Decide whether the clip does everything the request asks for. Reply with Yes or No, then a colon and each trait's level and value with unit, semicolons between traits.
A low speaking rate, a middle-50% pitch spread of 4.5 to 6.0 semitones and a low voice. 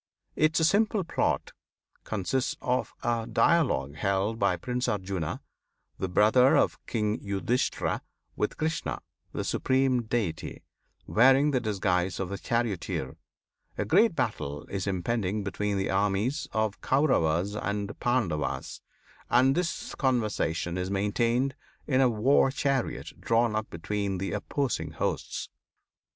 Yes: slow, 125 wpm; average, 5.1 semitones; low, 110 Hz